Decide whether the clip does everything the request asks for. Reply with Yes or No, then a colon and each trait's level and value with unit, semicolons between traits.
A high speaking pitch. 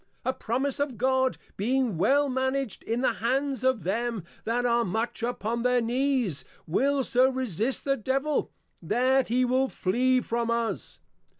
Yes: very high, 250 Hz